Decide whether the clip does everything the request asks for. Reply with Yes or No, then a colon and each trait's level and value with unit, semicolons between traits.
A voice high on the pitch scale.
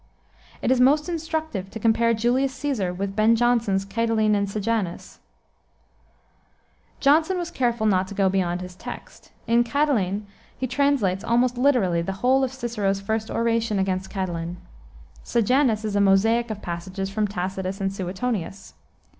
Yes: high, 215 Hz